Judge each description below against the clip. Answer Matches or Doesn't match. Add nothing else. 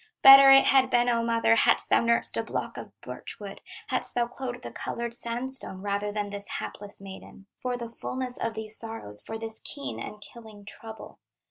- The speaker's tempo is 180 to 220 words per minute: Matches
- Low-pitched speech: Doesn't match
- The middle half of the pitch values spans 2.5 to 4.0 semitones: Matches